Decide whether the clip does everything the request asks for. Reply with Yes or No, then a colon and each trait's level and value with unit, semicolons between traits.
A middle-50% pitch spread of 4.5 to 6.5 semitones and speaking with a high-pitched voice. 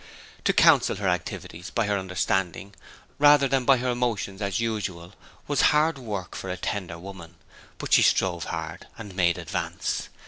No: average, 5.1 semitones; low, 100 Hz